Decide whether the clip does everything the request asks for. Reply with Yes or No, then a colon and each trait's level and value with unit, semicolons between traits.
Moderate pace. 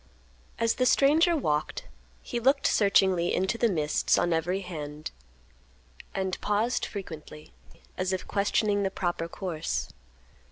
No: slow, 125 wpm